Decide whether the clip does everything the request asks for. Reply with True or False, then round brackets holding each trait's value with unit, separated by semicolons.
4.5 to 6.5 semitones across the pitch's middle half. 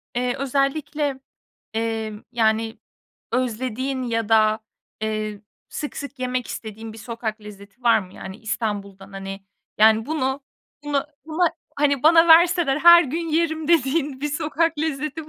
True (5.5 semitones)